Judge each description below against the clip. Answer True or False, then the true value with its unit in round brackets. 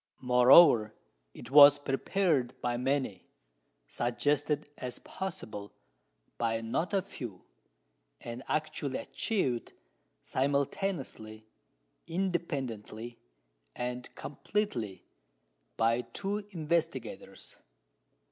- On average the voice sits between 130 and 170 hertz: True (135 Hz)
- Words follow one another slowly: True (75 wpm)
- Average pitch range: False (5.7 semitones)